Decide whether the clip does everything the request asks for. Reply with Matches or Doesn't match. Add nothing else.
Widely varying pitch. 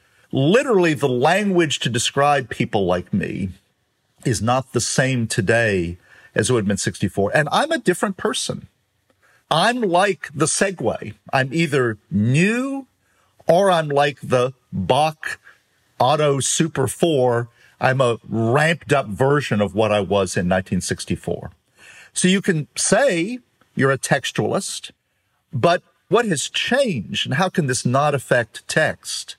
Matches